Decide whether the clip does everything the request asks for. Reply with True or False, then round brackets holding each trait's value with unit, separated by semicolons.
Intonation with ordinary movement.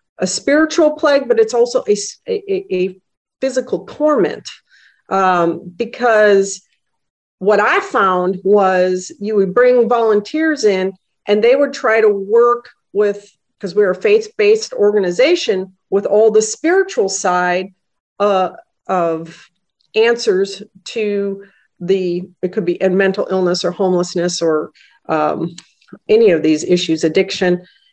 False (6.1 semitones)